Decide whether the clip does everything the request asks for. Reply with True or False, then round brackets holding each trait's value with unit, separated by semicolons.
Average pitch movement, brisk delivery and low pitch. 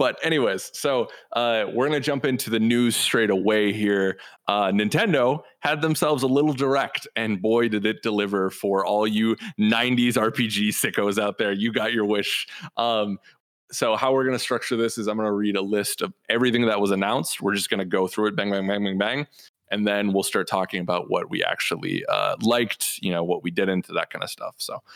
True (3.2 semitones; 210 wpm; 110 Hz)